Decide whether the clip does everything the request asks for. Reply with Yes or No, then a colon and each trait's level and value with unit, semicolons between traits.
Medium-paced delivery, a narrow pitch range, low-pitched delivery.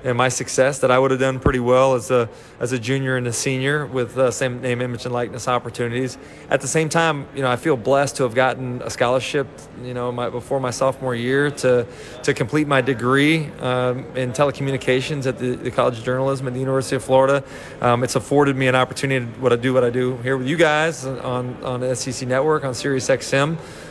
No: fast, 230 wpm; narrow, 1.6 semitones; low, 130 Hz